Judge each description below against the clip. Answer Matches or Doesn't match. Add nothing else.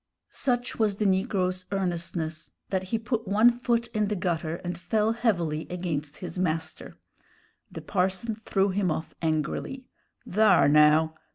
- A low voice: Doesn't match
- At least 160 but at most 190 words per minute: Doesn't match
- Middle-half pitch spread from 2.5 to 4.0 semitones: Doesn't match